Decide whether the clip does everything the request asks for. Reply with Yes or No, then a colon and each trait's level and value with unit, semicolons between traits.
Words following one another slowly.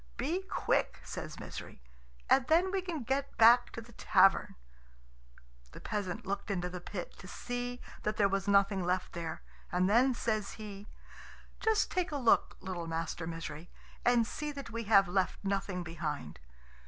No: average, 165 wpm